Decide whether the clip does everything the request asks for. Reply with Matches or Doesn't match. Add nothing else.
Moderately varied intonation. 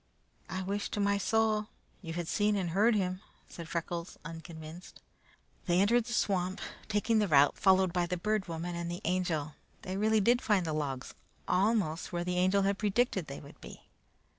Matches